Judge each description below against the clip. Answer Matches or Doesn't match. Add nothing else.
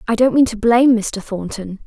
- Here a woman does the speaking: Matches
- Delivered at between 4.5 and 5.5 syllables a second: Matches